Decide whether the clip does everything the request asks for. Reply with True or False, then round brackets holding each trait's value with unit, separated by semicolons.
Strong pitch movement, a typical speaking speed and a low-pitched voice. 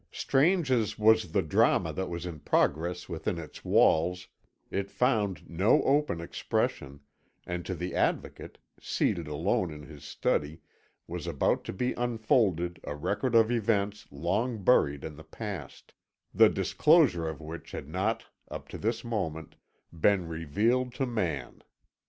True (5.9 semitones; 145 wpm; 95 Hz)